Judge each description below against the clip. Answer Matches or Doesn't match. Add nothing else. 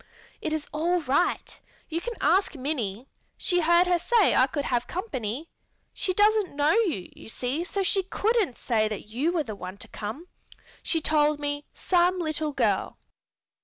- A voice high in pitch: Matches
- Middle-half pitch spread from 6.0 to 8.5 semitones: Doesn't match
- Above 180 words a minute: Doesn't match